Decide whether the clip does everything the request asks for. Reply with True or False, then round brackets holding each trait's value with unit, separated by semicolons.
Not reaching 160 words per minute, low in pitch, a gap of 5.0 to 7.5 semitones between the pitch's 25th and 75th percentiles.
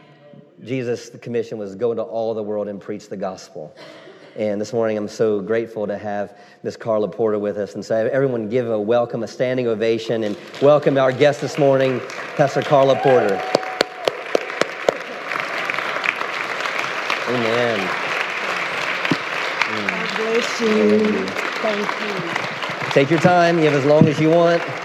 True (145 wpm; 125 Hz; 5.5 semitones)